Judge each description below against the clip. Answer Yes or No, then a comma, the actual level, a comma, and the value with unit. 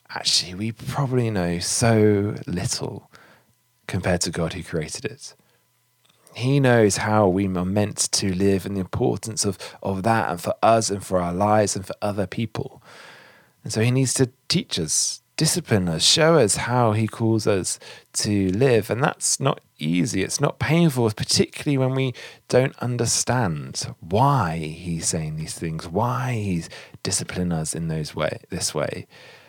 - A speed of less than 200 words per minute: Yes, average, 160 wpm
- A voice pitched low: Yes, low, 110 Hz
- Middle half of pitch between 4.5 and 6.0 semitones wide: Yes, average, 5.1 semitones